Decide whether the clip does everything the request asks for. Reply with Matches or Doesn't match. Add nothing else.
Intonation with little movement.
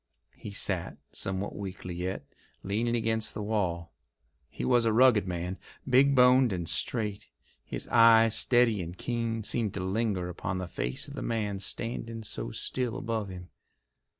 Doesn't match